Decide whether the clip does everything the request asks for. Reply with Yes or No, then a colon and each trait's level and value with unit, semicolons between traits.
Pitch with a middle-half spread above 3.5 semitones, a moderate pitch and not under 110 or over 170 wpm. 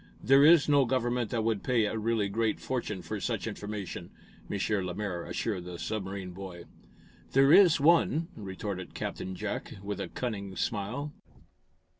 No: average, 4.8 semitones; low, 110 Hz; average, 150 wpm